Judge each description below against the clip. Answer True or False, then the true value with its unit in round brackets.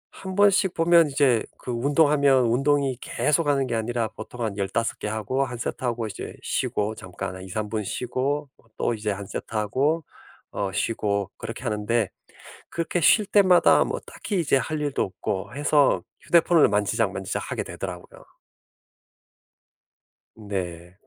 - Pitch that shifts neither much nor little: False (5.7 semitones)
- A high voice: False (120 Hz)